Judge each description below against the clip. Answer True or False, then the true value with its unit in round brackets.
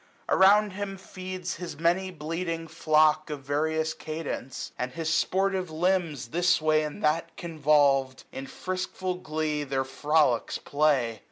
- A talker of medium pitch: True (160 Hz)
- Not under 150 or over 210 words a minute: False (135 wpm)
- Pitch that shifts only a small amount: False (3.5 semitones)